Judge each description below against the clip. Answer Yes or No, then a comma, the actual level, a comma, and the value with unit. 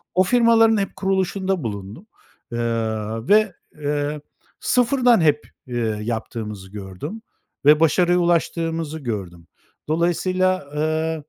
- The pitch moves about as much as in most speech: No, wide, 7.8 semitones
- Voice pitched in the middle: Yes, medium, 160 Hz